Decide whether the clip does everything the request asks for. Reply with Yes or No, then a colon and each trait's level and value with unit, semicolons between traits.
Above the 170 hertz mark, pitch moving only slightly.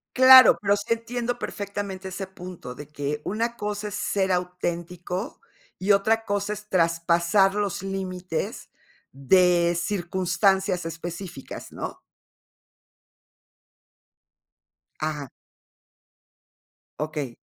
No: medium, 185 Hz; average, 3.1 semitones